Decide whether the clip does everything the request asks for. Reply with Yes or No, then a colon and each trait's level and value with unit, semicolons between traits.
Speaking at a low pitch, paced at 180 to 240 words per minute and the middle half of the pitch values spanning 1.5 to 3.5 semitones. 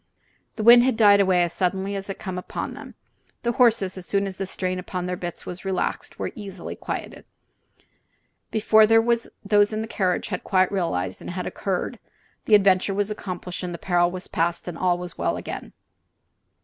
No: high, 190 Hz; average, 185 wpm; narrow, 2.6 semitones